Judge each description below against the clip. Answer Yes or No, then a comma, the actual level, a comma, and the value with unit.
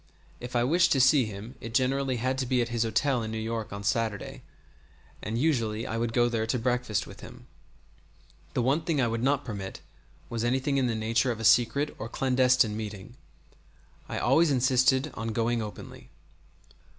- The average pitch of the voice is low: Yes, low, 120 Hz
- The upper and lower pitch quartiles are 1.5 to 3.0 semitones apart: Yes, average, 2.7 semitones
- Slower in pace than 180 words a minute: No, average, 185 wpm